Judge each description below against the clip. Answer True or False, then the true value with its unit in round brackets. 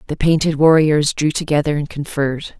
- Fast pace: False (160 wpm)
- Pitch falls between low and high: True (150 Hz)